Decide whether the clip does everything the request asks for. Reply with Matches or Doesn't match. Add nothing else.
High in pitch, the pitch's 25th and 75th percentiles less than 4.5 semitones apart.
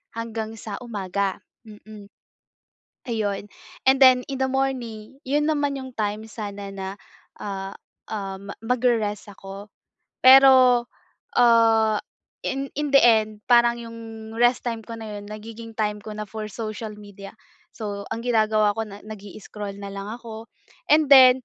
Matches